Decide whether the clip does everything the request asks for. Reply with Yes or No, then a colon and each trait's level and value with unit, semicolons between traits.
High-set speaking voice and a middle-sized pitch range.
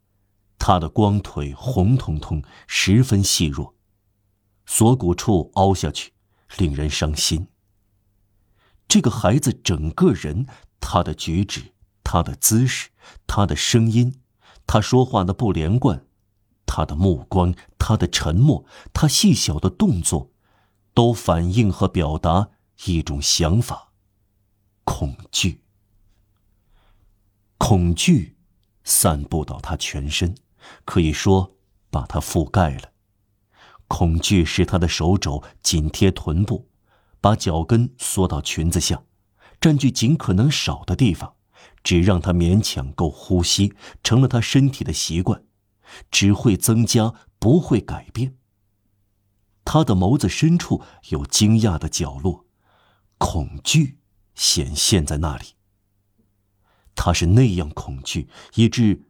No: low, 100 Hz; average, 3.4 semitones